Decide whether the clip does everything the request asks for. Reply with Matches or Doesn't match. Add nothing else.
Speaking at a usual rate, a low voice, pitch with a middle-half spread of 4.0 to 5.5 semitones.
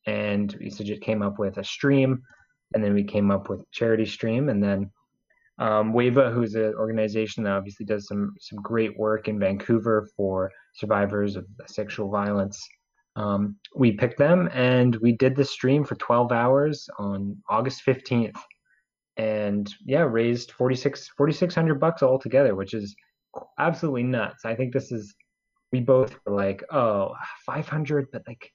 Matches